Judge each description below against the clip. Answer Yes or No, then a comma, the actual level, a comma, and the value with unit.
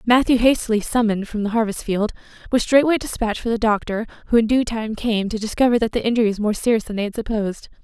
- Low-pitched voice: No, high, 225 Hz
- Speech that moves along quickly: Yes, fast, 230 wpm